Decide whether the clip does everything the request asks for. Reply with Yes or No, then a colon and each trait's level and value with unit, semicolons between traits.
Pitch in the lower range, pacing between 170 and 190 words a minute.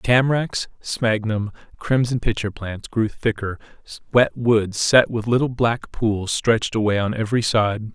No: low, 115 Hz; average, 145 wpm